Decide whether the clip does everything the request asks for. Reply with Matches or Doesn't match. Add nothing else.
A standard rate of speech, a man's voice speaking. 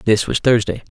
Matches